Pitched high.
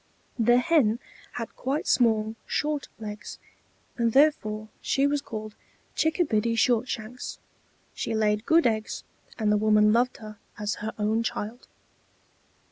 Yes: high, 225 Hz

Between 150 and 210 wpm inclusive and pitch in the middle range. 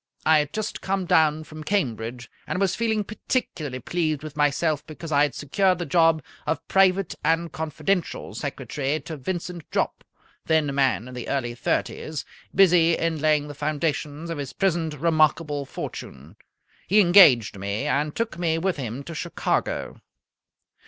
Yes: average, 160 wpm; medium, 155 Hz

